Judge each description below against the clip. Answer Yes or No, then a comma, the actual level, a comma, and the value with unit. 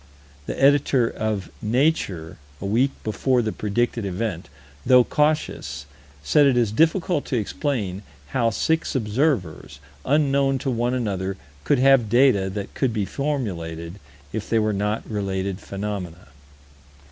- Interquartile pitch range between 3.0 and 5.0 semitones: No, wide, 5.6 semitones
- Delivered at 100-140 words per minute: Yes, slow, 135 wpm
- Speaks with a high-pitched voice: No, low, 110 Hz